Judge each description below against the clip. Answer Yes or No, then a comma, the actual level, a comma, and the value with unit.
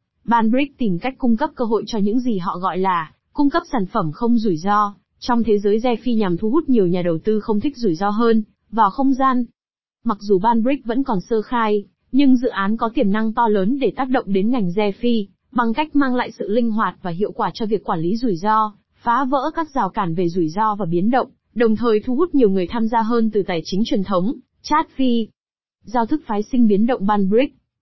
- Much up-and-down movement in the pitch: No, average, 3.5 semitones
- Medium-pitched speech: No, high, 225 Hz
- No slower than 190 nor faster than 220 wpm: No, average, 240 wpm